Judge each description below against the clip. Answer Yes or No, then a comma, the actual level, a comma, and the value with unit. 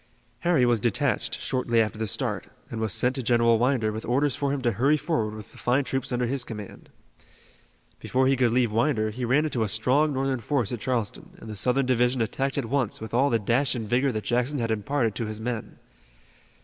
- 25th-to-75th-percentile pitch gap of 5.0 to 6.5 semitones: No, average, 3.1 semitones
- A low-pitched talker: Yes, low, 120 Hz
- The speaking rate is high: Yes, fast, 220 wpm